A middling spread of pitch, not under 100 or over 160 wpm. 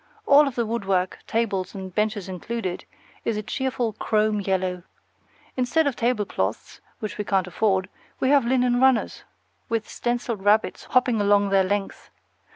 Yes: average, 3.8 semitones; average, 150 wpm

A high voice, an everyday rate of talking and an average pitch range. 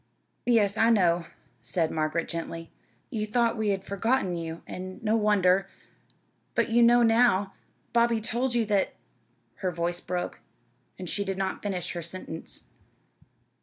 Yes: high, 195 Hz; average, 150 wpm; average, 4.3 semitones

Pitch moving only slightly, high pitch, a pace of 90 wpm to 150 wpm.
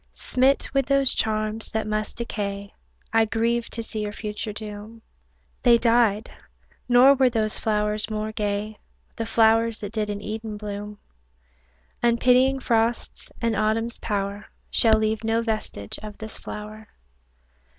Yes: narrow, 1.6 semitones; high, 220 Hz; average, 140 wpm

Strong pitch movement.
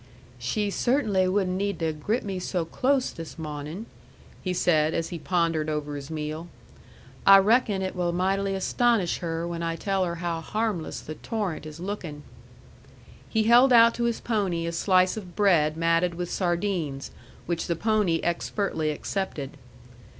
No: average, 3.7 semitones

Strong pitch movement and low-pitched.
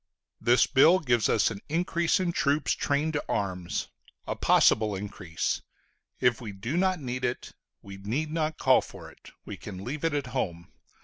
Yes: wide, 7.3 semitones; low, 125 Hz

